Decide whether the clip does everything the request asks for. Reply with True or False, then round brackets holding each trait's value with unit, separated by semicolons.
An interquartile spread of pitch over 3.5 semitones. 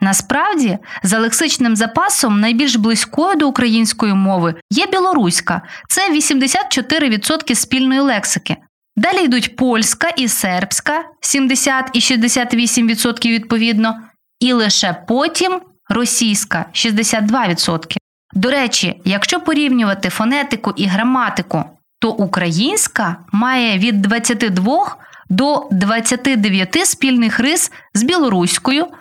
True (4.8 semitones)